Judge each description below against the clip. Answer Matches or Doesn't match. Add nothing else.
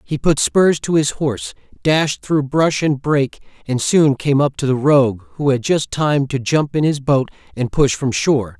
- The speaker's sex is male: Matches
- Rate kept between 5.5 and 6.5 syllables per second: Doesn't match